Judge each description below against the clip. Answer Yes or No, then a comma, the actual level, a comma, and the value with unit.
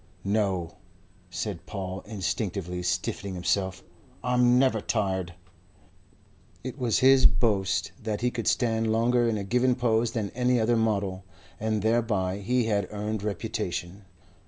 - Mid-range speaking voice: No, low, 105 Hz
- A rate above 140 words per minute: No, slow, 135 wpm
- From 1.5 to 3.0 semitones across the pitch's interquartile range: No, average, 3.7 semitones